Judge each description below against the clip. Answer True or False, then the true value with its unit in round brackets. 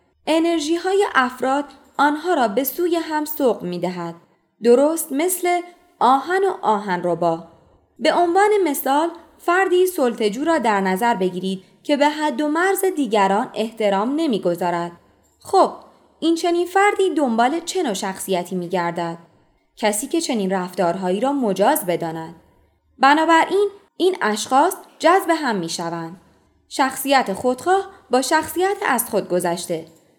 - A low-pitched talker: False (270 Hz)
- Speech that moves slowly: False (130 wpm)